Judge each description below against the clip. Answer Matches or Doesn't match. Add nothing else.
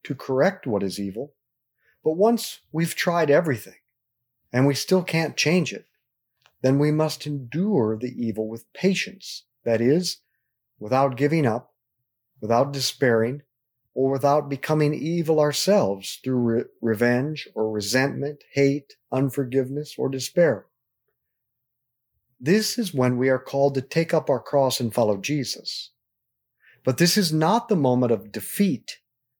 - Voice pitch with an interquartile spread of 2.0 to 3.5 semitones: Doesn't match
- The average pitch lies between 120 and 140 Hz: Matches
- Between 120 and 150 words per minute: Matches